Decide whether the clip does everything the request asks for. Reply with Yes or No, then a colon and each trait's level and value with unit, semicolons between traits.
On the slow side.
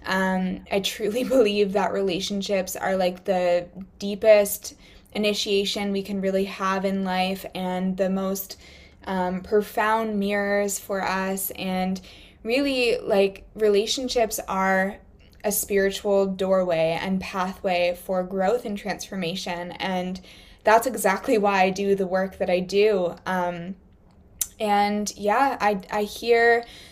Yes: slow, 125 wpm